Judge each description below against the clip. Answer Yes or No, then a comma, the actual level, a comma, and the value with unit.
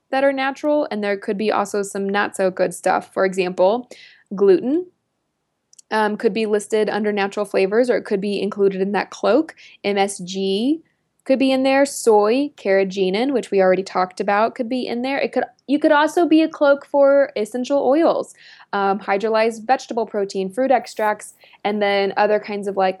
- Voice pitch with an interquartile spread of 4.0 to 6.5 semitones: Yes, average, 5.2 semitones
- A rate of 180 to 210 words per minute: Yes, average, 185 wpm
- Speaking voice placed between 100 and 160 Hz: No, high, 210 Hz